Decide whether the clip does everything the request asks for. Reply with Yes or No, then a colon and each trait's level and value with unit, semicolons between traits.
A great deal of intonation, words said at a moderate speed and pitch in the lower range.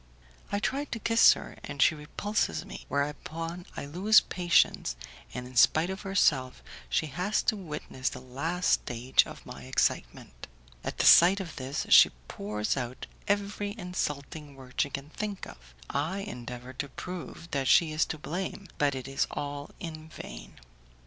No: wide, 5.8 semitones; average, 165 wpm; medium, 150 Hz